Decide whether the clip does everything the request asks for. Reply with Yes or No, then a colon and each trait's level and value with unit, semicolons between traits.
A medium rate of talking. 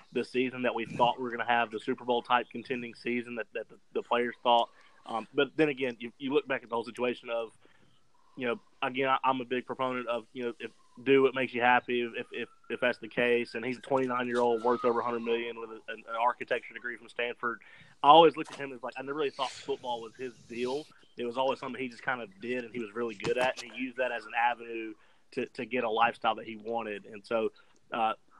No: fast, 260 wpm